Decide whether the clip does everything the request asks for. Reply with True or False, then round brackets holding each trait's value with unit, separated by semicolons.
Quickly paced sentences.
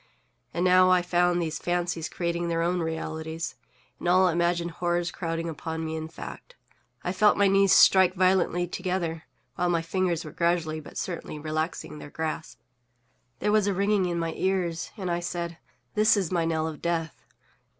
False (175 wpm)